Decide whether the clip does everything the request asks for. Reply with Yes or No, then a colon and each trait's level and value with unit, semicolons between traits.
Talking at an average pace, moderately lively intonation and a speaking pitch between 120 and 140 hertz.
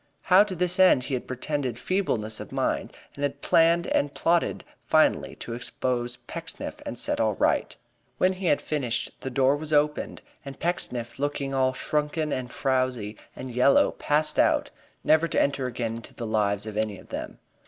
Yes: average, 180 wpm; average, 4.0 semitones; low, 135 Hz